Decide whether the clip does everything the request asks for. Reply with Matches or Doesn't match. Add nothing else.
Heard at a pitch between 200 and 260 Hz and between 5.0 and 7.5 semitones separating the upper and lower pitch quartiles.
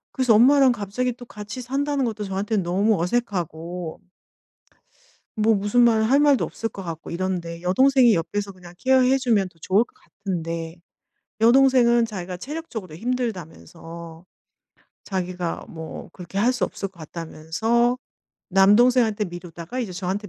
Matches